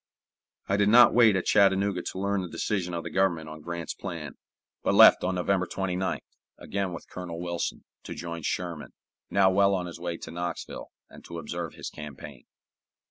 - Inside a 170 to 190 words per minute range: Yes, average, 185 wpm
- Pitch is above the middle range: No, very low, 90 Hz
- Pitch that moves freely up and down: No, narrow, 2.4 semitones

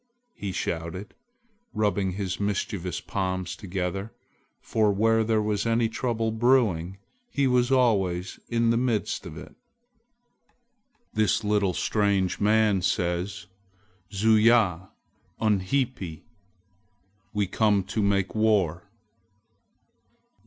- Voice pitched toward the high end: No, low, 105 Hz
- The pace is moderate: No, slow, 100 wpm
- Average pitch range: Yes, average, 3.1 semitones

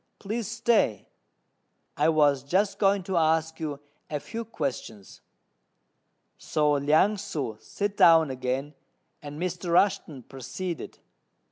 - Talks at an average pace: No, slow, 115 wpm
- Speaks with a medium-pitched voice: Yes, medium, 160 Hz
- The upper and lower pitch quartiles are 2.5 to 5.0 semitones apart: No, wide, 5.6 semitones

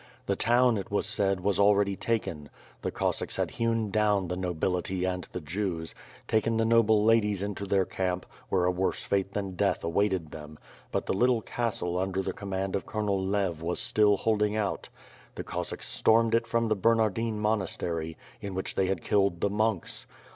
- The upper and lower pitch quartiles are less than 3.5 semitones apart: Yes, average, 2.8 semitones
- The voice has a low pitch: Yes, low, 100 Hz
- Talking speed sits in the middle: Yes, average, 185 wpm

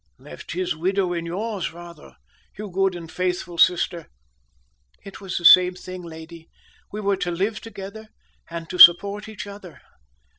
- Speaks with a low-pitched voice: No, medium, 180 Hz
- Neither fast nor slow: Yes, average, 155 wpm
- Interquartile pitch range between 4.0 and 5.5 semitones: No, narrow, 2.6 semitones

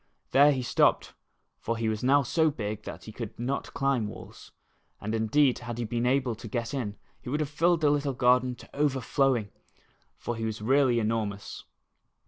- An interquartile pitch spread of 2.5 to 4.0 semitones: Yes, average, 3.7 semitones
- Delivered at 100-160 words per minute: No, average, 185 wpm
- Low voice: Yes, low, 125 Hz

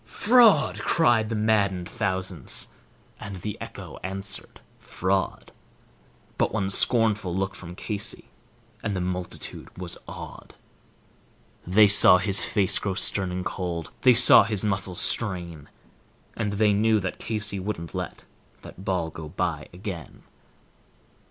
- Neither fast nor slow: No, slow, 130 wpm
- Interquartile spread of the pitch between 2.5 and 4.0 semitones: Yes, average, 2.8 semitones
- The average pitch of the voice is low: Yes, very low, 95 Hz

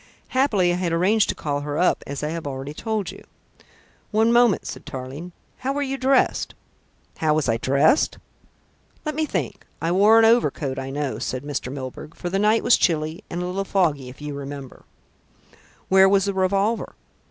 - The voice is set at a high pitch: No, medium, 175 Hz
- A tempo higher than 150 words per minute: Yes, average, 190 wpm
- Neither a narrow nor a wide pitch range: No, wide, 6.7 semitones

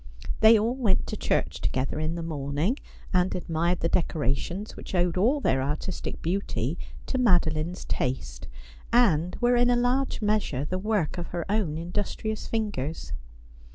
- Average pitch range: No, wide, 5.7 semitones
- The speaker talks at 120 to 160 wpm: Yes, average, 155 wpm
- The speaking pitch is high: No, medium, 180 Hz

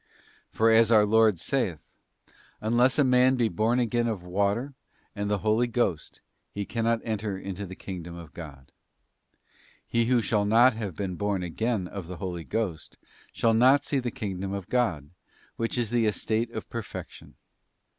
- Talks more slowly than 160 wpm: No, average, 175 wpm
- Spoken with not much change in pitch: No, average, 3.8 semitones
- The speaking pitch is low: Yes, low, 110 Hz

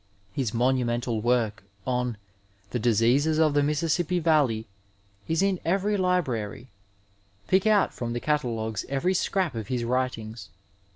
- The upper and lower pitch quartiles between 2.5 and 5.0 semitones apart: No, wide, 5.6 semitones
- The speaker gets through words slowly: Yes, slow, 130 wpm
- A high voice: No, low, 130 Hz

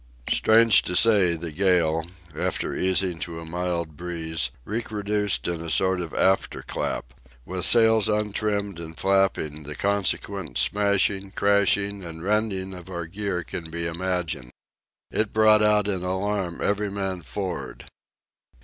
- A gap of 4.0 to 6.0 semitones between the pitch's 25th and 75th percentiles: No, average, 3.2 semitones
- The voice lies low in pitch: Yes, very low, 95 Hz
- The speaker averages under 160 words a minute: Yes, average, 140 wpm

